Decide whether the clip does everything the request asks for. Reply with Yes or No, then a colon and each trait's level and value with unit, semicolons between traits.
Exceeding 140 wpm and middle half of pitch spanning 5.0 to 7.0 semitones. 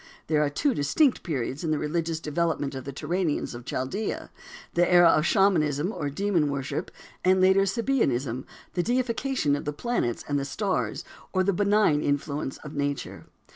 Yes: average, 170 wpm; wide, 5.4 semitones